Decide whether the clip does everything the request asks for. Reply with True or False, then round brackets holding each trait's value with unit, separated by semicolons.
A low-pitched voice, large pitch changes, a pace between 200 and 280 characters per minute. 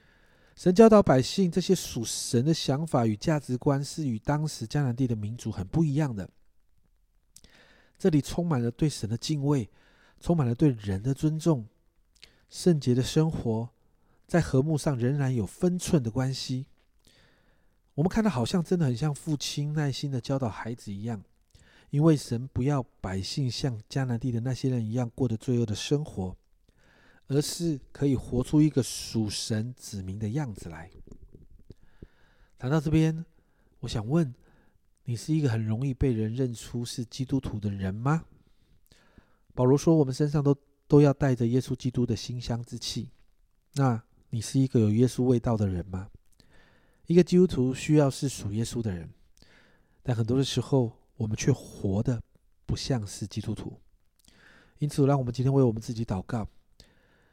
False (125 Hz; 4.9 semitones; 240 characters per minute)